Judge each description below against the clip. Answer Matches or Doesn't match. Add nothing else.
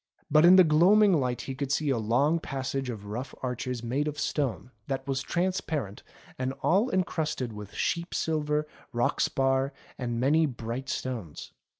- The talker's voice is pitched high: Doesn't match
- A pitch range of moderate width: Matches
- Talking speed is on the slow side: Doesn't match